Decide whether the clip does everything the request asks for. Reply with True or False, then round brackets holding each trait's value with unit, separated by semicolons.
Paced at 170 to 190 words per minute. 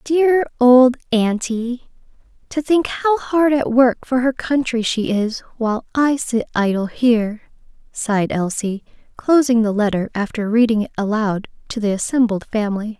False (150 wpm)